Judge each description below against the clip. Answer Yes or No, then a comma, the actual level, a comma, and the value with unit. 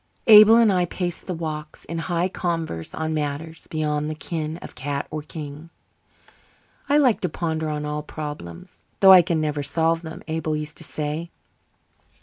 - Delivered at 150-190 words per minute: Yes, average, 170 wpm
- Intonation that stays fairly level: Yes, narrow, 2.2 semitones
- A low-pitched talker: No, medium, 160 Hz